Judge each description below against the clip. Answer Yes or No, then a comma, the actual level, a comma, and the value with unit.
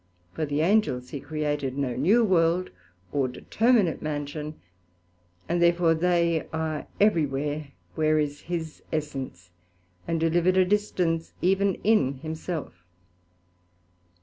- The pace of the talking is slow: Yes, slow, 120 wpm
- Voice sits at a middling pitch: Yes, medium, 160 Hz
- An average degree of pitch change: Yes, average, 3.3 semitones